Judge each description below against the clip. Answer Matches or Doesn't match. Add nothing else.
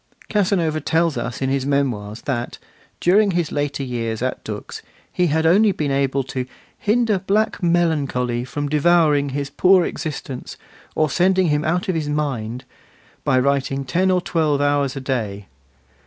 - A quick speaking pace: Doesn't match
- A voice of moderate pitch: Matches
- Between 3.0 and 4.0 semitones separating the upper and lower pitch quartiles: Doesn't match